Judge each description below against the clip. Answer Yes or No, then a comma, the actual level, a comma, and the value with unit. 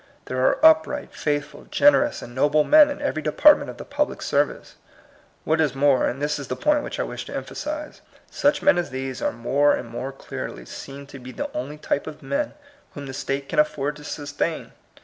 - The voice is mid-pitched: Yes, medium, 145 Hz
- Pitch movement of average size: Yes, average, 4.1 semitones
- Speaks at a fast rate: Yes, fast, 210 wpm